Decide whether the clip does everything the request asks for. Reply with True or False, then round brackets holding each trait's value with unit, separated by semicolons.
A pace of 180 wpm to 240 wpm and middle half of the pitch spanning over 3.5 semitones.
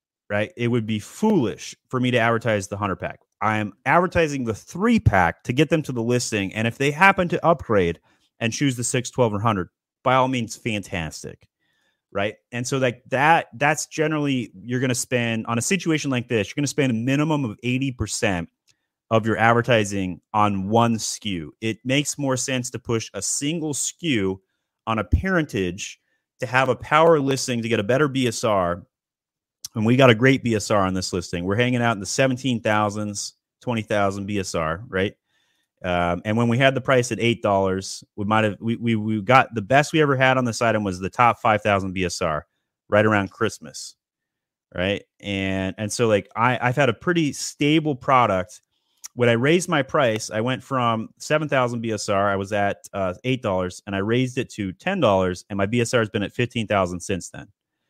True (195 wpm; 4.3 semitones)